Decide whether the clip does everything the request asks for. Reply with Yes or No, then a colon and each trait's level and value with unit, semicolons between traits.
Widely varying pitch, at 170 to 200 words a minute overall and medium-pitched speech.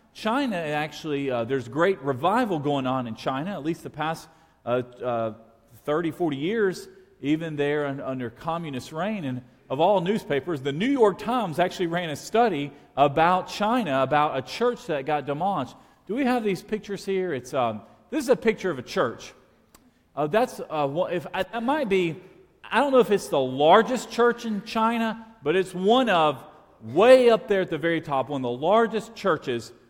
Yes: wide, 7.3 semitones; average, 185 wpm; medium, 175 Hz